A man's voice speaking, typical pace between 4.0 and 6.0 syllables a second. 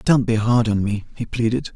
Yes: male; 5.2 syllables/s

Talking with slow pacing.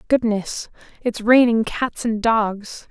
Yes: slow, 125 wpm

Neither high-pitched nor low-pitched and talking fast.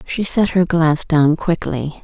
No: medium, 165 Hz; average, 175 wpm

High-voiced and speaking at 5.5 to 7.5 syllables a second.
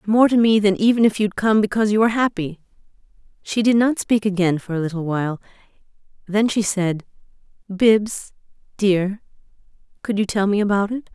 Yes: high, 205 Hz; 5.6 syllables/s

